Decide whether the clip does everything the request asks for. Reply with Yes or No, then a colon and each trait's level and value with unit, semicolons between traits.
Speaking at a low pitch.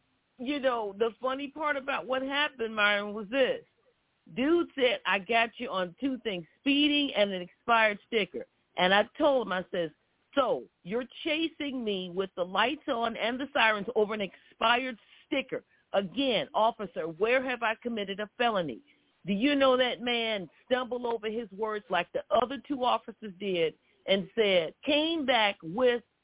No: high, 230 Hz